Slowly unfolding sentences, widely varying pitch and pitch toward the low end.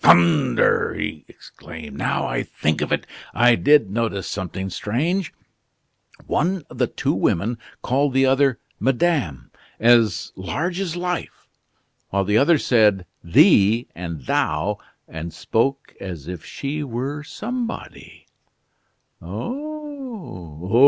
Yes: slow, 120 wpm; wide, 8.8 semitones; low, 115 Hz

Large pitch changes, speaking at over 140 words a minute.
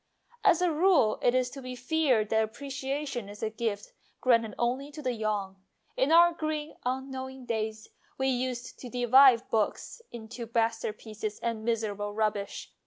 No: average, 3.5 semitones; average, 165 wpm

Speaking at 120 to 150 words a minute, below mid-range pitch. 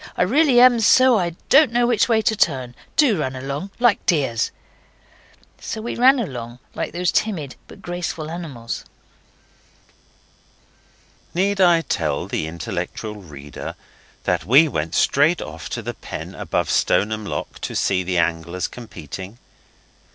No: average, 145 wpm; medium, 150 Hz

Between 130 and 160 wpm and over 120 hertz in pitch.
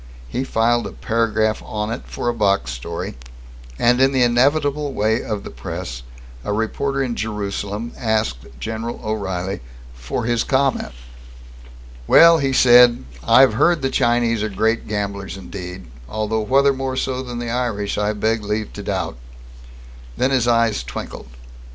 No: average, 150 wpm; low, 115 Hz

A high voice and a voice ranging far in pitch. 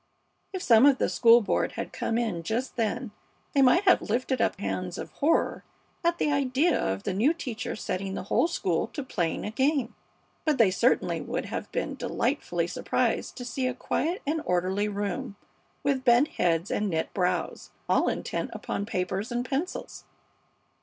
Yes: high, 235 Hz; wide, 5.7 semitones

